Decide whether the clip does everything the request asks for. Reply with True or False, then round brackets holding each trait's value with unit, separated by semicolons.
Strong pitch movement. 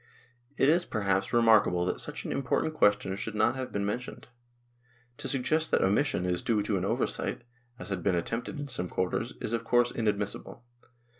False (4.1 semitones)